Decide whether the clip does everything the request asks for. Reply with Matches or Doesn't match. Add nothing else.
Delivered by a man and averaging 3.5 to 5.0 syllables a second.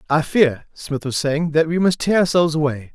Doesn't match